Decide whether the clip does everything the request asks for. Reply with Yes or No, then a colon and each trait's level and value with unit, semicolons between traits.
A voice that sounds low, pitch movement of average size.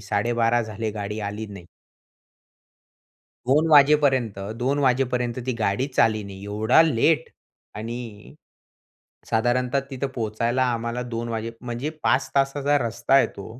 Yes: low, 120 Hz; average, 3.6 semitones